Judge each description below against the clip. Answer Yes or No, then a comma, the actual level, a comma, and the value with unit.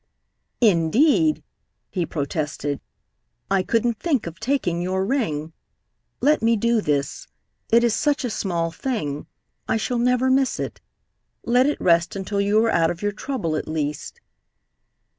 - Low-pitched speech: No, high, 205 Hz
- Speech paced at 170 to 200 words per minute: No, average, 145 wpm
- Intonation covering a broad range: Yes, wide, 6.9 semitones